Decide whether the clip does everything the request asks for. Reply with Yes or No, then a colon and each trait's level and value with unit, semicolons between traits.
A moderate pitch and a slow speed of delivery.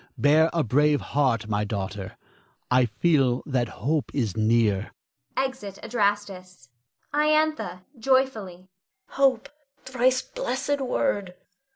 Yes: medium, 180 Hz; slow, 100 wpm